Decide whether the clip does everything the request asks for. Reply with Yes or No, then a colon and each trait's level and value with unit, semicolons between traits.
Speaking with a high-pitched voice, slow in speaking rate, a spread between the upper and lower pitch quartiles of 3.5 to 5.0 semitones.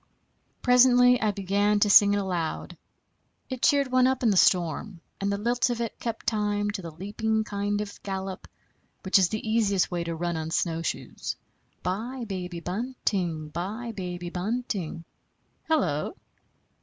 No: high, 205 Hz; average, 155 wpm; average, 4.4 semitones